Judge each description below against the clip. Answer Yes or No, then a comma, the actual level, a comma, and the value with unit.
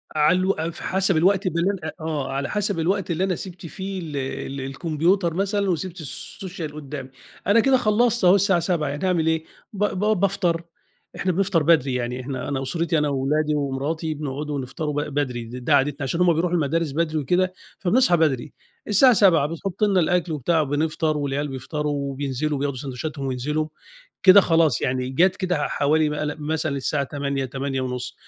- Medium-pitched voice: Yes, medium, 155 Hz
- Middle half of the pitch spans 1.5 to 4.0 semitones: No, average, 4.4 semitones